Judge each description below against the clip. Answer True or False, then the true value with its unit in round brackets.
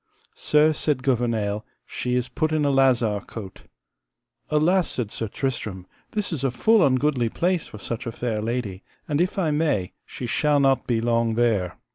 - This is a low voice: True (125 Hz)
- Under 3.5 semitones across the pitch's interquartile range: False (5.0 semitones)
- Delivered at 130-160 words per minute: False (175 wpm)